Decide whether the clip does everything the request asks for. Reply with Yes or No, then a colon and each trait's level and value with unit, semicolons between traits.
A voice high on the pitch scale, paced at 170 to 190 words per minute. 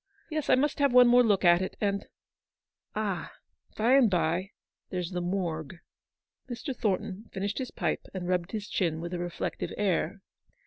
Yes: high, 195 Hz; average, 180 wpm